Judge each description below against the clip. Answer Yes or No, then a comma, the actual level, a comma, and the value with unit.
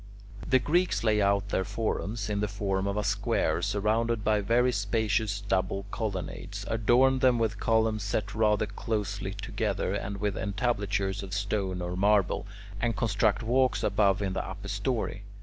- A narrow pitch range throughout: Yes, narrow, 2.1 semitones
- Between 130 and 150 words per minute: No, average, 160 wpm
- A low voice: Yes, low, 105 Hz